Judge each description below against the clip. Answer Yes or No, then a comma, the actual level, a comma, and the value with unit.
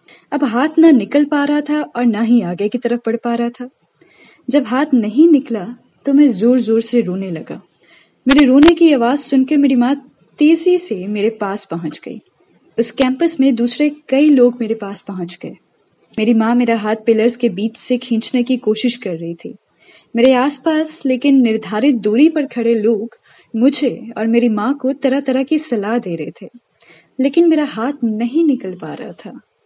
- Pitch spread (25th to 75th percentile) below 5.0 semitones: Yes, average, 3.9 semitones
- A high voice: Yes, high, 245 Hz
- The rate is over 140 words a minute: Yes, fast, 190 wpm